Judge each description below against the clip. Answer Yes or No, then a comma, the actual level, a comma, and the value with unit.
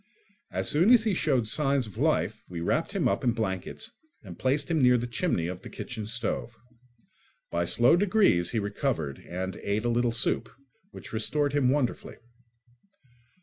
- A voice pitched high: No, low, 120 Hz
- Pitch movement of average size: No, wide, 6.2 semitones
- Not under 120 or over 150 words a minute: No, average, 170 wpm